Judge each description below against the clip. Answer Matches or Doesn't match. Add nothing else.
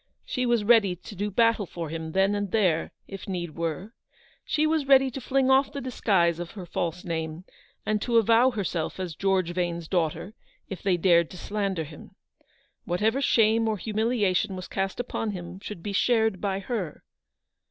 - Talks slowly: Doesn't match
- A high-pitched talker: Matches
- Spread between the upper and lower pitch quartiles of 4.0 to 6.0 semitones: Matches